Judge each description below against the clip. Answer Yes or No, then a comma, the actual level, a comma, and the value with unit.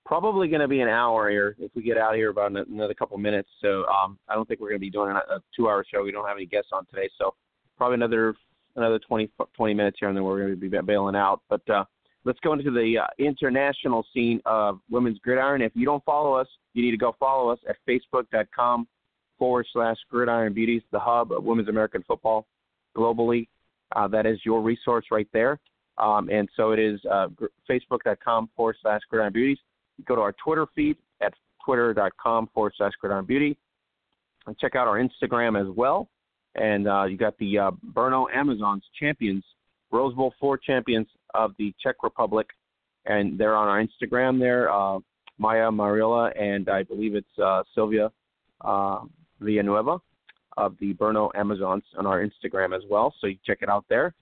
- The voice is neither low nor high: No, low, 110 Hz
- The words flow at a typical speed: Yes, average, 195 wpm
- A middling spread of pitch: Yes, average, 3.0 semitones